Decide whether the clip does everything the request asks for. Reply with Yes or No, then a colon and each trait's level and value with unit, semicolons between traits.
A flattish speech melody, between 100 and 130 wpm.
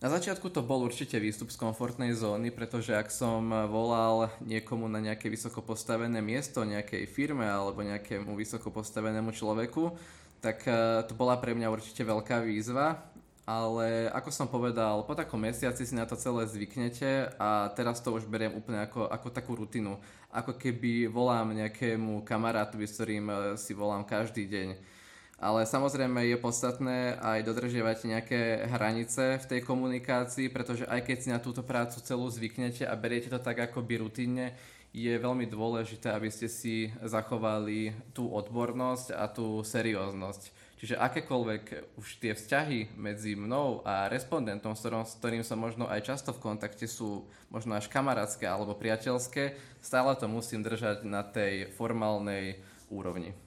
No: narrow, 2.3 semitones; average, 150 wpm